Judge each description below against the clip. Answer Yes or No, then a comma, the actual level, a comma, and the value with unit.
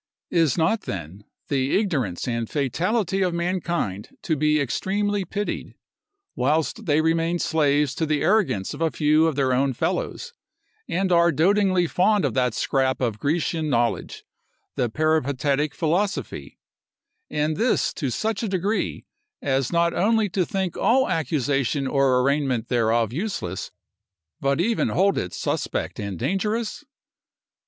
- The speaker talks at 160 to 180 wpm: No, average, 140 wpm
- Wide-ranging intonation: Yes, wide, 6.0 semitones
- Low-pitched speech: No, medium, 155 Hz